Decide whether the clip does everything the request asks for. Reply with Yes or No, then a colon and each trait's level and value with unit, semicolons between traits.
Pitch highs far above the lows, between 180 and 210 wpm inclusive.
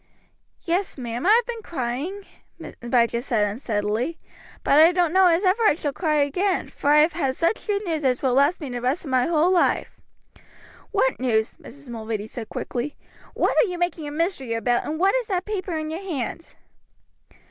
Yes: wide, 6.4 semitones; average, 200 wpm